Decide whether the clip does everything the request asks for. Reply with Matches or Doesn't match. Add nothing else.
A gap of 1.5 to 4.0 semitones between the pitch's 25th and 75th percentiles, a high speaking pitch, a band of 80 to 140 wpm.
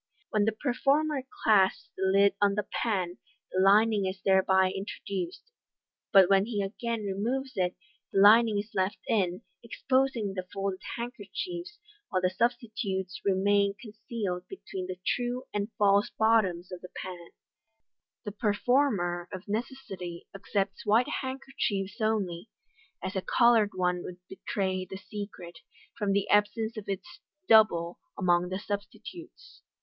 Matches